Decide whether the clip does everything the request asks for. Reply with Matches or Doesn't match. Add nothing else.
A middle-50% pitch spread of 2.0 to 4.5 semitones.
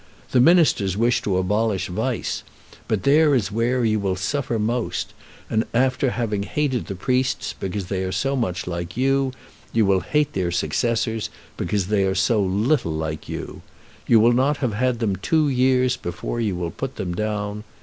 Doesn't match